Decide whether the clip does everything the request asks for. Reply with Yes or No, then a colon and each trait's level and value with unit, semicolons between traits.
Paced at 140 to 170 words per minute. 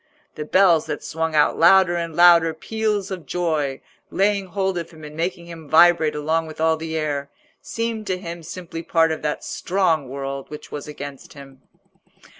No: average, 180 wpm